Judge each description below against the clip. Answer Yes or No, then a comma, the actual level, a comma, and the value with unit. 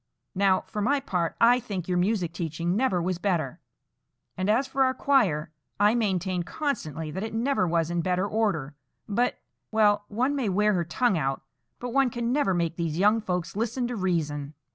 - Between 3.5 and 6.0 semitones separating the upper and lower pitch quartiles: Yes, average, 5.2 semitones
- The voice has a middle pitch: No, high, 195 Hz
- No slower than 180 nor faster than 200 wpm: Yes, average, 185 wpm